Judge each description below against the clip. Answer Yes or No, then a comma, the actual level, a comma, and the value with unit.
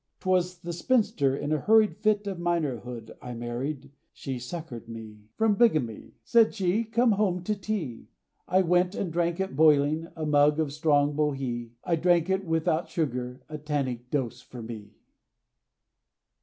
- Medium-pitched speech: Yes, medium, 155 Hz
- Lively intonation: Yes, wide, 5.9 semitones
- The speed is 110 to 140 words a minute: No, average, 155 wpm